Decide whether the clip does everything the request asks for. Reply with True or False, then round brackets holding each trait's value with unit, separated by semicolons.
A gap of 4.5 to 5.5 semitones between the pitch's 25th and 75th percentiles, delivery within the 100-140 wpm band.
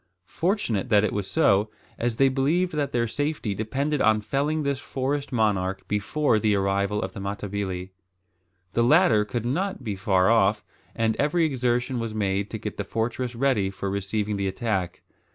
False (5.1 semitones; 170 wpm)